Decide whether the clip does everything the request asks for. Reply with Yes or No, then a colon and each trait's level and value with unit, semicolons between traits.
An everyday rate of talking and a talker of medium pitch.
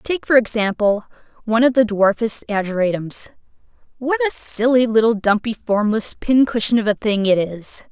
No: average, 150 wpm; high, 225 Hz